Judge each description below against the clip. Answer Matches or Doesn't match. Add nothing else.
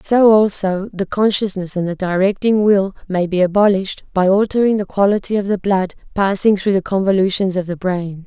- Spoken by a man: Doesn't match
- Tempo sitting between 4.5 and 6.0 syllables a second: Matches